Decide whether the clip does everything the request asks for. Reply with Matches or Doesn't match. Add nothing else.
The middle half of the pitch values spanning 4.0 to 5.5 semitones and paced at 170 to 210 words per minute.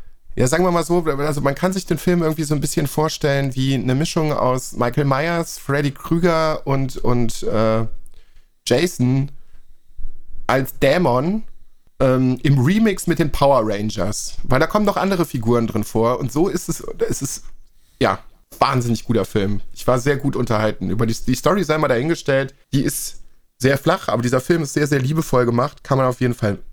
Matches